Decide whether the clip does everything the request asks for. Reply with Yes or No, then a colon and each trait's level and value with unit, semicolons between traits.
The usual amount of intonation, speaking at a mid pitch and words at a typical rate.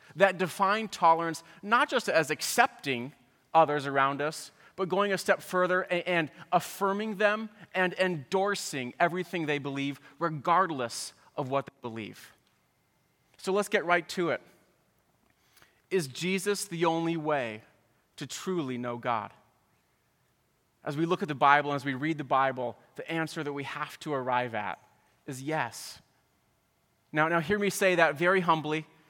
Yes: average, 4.6 semitones; medium, 165 Hz; average, 150 wpm